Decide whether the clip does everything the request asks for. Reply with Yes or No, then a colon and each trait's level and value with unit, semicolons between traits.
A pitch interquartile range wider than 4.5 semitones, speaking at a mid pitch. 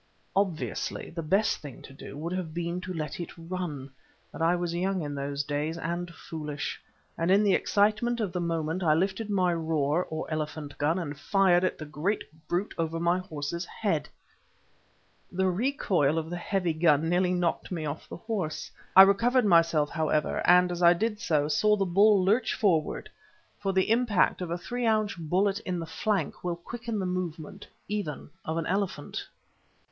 No: average, 3.7 semitones; medium, 175 Hz